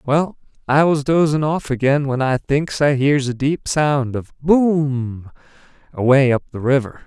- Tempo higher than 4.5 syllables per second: No, 4.1 syllables/s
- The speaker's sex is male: Yes, male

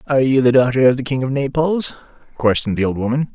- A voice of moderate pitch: No, low, 130 Hz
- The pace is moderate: No, fast, 235 wpm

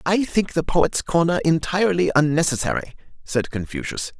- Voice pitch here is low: No, medium, 155 Hz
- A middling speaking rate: No, slow, 130 wpm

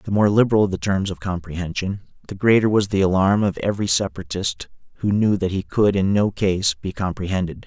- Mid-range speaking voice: No, low, 100 Hz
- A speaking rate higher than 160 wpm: Yes, average, 195 wpm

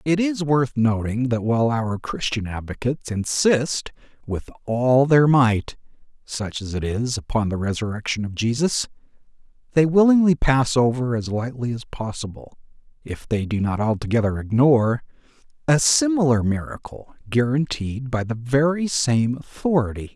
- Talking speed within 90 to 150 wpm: Yes, slow, 135 wpm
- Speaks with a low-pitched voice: Yes, low, 125 Hz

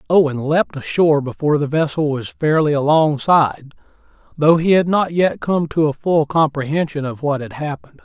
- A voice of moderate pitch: Yes, medium, 150 Hz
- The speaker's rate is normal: Yes, average, 170 wpm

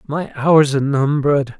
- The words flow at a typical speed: Yes, average, 150 wpm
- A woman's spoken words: No, male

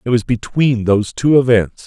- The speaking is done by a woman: No, male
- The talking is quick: No, average, 195 wpm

